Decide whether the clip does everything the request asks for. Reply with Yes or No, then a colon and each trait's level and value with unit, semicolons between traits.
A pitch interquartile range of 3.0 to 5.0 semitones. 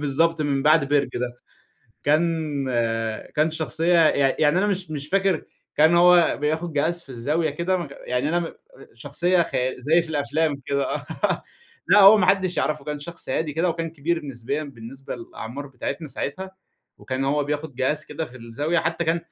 Yes: average, 3.3 semitones